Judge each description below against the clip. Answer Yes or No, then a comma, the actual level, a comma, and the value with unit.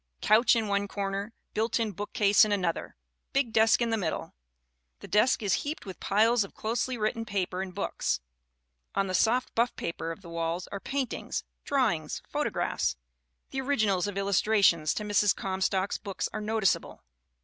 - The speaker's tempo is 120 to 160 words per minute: No, average, 170 wpm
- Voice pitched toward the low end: No, high, 205 Hz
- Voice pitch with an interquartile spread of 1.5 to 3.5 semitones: Yes, average, 2.8 semitones